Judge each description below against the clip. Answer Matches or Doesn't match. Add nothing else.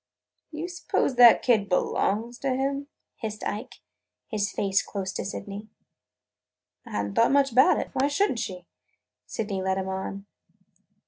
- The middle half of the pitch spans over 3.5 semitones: Matches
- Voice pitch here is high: Matches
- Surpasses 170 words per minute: Doesn't match